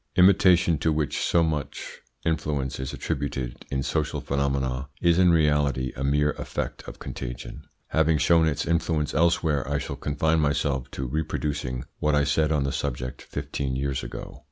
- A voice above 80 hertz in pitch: No, very low, 75 Hz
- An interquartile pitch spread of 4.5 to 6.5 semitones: No, average, 2.8 semitones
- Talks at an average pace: Yes, average, 160 wpm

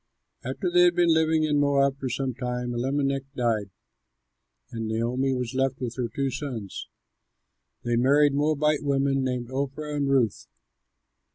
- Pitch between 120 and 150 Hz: Yes, low, 135 Hz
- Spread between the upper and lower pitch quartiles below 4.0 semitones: Yes, average, 2.7 semitones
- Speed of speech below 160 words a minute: Yes, average, 150 wpm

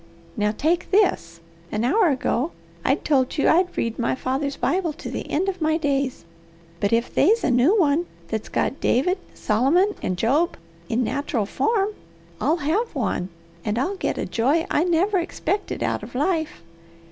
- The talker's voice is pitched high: Yes, very high, 290 Hz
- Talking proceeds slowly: No, average, 170 wpm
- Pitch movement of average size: No, wide, 6.6 semitones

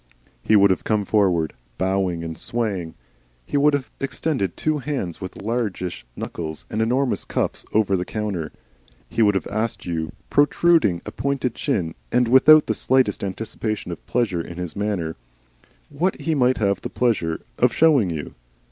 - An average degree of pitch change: No, wide, 6.1 semitones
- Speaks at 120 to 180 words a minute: Yes, average, 165 wpm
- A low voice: Yes, low, 105 Hz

